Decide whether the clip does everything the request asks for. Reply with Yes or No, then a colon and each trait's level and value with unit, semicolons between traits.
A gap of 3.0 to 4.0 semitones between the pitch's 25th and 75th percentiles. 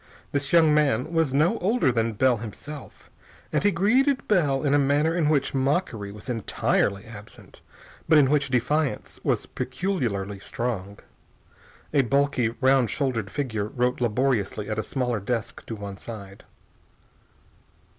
No: average, 5.1 semitones